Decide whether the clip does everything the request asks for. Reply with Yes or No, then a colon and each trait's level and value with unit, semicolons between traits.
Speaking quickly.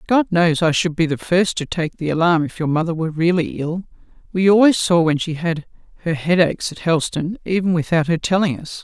Yes: fast, 215 wpm